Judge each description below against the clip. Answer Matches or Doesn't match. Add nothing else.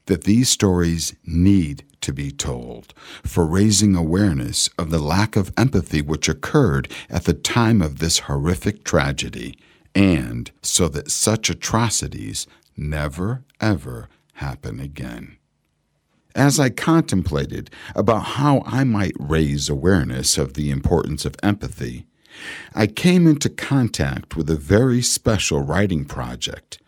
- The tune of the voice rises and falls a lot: Matches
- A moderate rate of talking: Doesn't match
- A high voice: Doesn't match